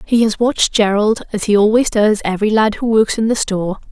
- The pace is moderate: No, fast, 230 wpm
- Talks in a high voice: Yes, high, 215 Hz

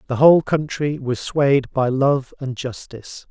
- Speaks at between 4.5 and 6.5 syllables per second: No, 4.2 syllables/s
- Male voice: Yes, male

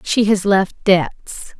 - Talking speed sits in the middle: Yes, average, 150 wpm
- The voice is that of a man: No, female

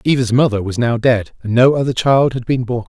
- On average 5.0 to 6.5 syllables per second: Yes, 5.6 syllables/s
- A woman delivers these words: No, male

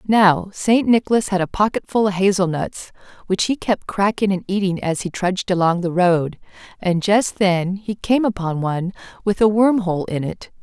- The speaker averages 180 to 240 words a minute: Yes, average, 190 wpm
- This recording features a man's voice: No, female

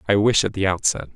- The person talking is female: No, male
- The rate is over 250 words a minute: Yes, fast, 260 wpm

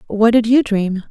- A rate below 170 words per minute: No, fast, 215 wpm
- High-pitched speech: Yes, high, 220 Hz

